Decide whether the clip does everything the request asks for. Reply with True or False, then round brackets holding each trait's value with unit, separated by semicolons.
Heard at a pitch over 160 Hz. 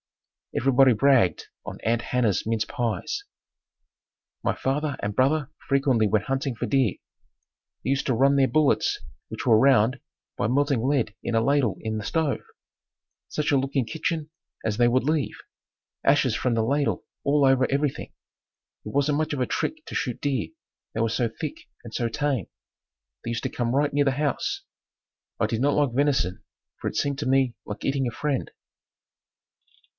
False (135 Hz)